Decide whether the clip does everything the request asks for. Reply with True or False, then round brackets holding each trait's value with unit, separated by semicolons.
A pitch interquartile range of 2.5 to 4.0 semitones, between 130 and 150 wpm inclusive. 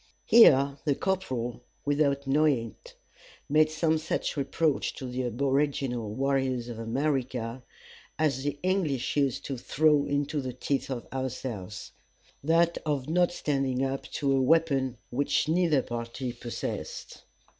True (3.1 semitones; 135 wpm)